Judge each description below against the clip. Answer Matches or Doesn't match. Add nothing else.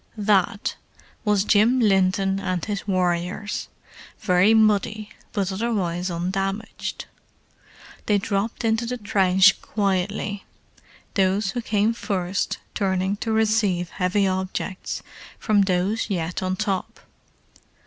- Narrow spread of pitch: Matches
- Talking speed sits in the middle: Doesn't match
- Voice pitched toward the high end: Matches